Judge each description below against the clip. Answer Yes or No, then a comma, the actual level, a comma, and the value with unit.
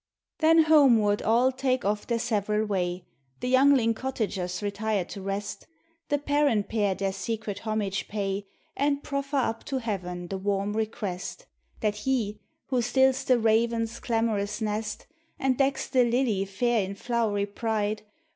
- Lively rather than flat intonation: No, average, 3.9 semitones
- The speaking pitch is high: Yes, high, 220 Hz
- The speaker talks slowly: No, average, 145 wpm